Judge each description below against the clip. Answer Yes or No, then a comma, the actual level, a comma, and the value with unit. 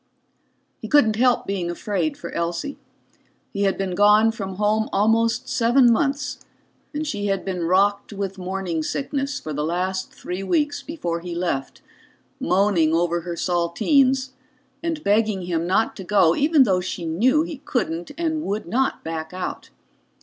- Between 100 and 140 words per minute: No, average, 155 wpm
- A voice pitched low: No, high, 200 Hz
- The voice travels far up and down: Yes, wide, 6.5 semitones